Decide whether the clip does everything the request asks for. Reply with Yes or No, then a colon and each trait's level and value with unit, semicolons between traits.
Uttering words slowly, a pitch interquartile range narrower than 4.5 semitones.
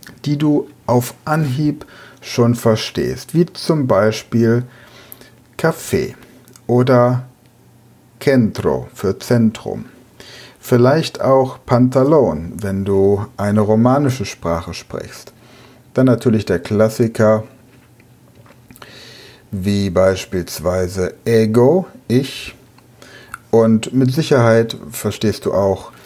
Yes: slow, 85 wpm; average, 2.9 semitones